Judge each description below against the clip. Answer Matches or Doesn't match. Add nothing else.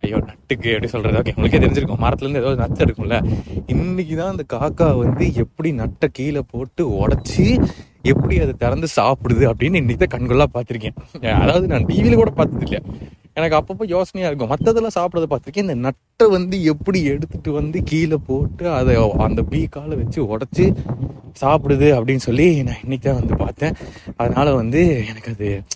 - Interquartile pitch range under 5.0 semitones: Doesn't match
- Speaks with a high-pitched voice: Doesn't match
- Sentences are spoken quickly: Matches